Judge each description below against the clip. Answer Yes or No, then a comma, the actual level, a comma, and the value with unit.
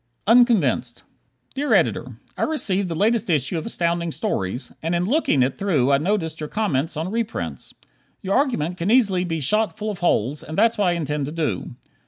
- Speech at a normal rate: Yes, average, 190 wpm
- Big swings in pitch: Yes, wide, 6.0 semitones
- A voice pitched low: No, medium, 175 Hz